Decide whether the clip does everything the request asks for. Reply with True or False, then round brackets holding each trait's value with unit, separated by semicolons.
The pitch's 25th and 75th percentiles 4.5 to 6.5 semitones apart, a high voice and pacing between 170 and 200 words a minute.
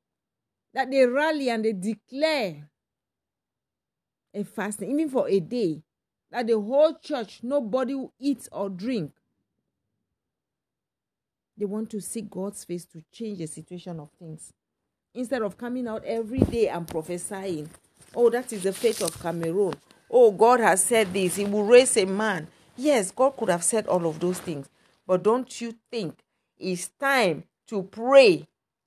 False (5.6 semitones; 215 Hz; 155 wpm)